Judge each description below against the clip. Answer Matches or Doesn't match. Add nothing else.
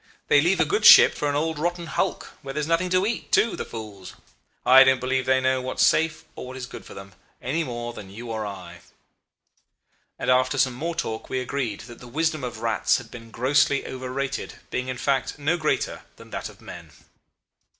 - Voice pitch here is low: Matches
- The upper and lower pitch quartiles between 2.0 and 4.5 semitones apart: Matches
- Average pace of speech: Doesn't match